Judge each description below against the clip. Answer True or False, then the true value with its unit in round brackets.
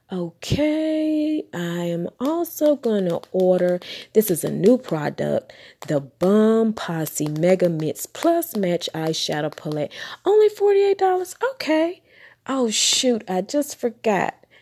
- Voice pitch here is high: True (215 Hz)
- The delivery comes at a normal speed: False (115 wpm)